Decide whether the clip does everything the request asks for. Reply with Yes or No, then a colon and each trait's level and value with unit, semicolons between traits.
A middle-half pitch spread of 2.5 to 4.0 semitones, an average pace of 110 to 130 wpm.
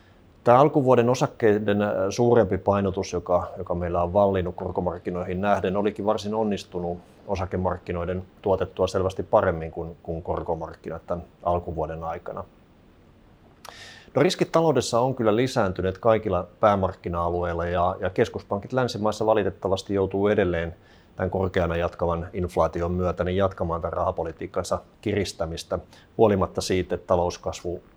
Yes: average, 2.9 semitones; average, 115 wpm